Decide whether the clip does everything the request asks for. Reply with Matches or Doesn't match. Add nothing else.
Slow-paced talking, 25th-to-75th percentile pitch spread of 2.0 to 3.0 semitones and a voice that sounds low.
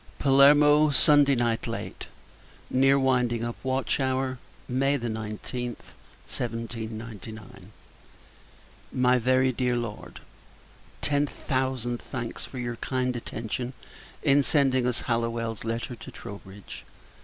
Matches